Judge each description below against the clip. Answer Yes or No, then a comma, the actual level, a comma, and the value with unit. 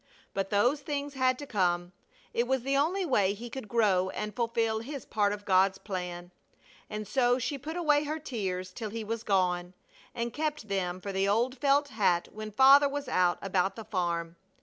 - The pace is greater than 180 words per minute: Yes, average, 195 wpm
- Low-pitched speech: No, high, 220 Hz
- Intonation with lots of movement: Yes, wide, 5.8 semitones